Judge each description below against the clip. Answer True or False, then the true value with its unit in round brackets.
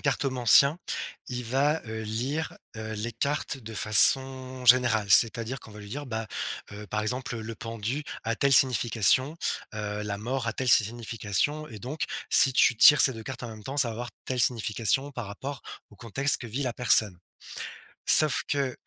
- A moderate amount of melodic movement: True (3.4 semitones)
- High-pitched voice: False (120 Hz)